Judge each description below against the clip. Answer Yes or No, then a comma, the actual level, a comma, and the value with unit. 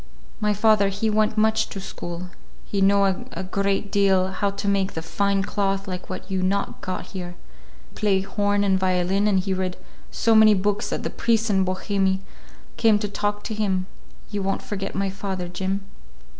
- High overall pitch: Yes, high, 195 Hz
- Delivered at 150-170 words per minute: No, average, 185 wpm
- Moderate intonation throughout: No, narrow, 1.5 semitones